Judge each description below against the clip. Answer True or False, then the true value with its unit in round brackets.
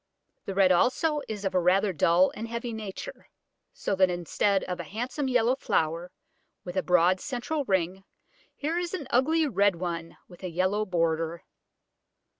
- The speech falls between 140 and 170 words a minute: True (165 wpm)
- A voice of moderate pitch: False (195 Hz)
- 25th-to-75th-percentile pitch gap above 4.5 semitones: True (5.5 semitones)